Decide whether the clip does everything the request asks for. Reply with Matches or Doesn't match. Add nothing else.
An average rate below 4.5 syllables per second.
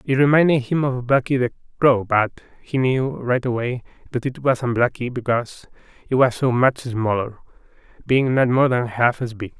Doesn't match